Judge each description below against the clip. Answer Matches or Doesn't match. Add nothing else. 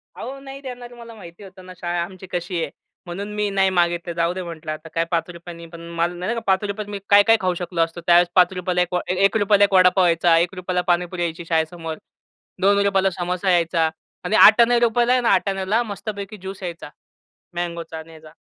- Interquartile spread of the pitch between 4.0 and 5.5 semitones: Doesn't match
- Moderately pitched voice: Matches